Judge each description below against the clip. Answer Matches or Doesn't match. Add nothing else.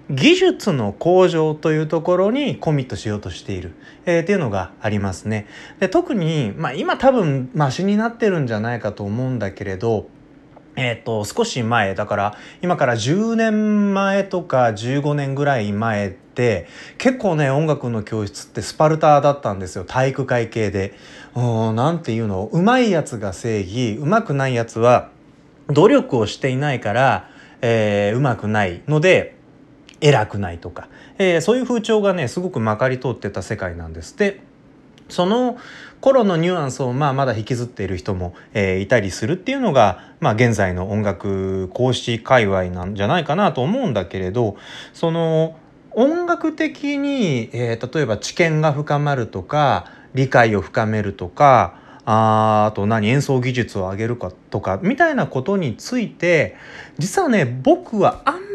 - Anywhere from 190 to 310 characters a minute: Doesn't match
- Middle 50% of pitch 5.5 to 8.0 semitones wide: Doesn't match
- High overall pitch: Doesn't match